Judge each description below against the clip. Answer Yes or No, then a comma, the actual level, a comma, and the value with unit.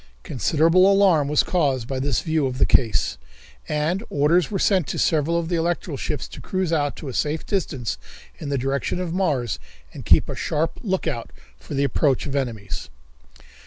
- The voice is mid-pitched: Yes, medium, 150 Hz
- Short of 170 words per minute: No, average, 185 wpm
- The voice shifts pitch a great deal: No, average, 4.0 semitones